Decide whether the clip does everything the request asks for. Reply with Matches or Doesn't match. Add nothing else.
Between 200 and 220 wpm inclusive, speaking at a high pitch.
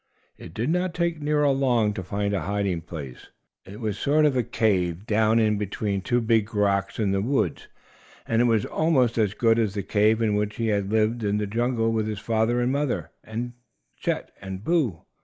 Doesn't match